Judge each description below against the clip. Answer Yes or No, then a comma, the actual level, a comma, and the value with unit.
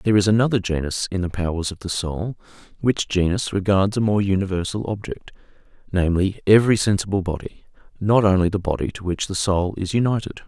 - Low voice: Yes, very low, 95 Hz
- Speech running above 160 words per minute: Yes, average, 170 wpm